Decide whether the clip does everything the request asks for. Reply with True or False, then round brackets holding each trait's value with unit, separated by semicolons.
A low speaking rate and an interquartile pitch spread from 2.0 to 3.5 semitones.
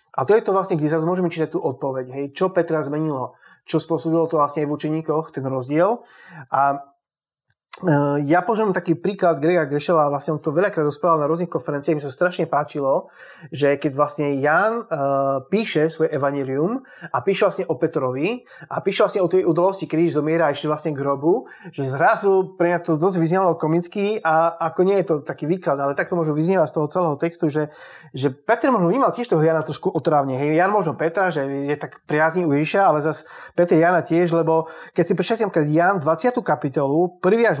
False (205 wpm; 3.2 semitones)